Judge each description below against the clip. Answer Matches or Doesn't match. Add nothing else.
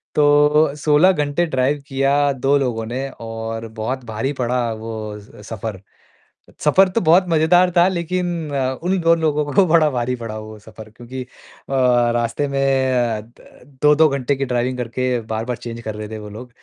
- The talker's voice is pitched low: Matches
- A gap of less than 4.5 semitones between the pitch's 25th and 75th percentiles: Doesn't match